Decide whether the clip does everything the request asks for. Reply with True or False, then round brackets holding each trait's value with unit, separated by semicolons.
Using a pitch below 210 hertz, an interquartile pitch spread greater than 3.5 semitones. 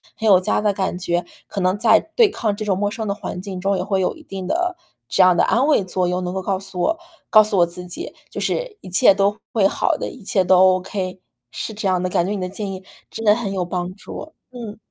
False (195 Hz; 2.7 semitones)